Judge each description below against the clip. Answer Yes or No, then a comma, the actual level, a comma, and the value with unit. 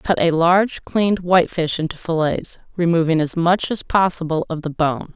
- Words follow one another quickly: No, average, 175 wpm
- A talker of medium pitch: Yes, medium, 170 Hz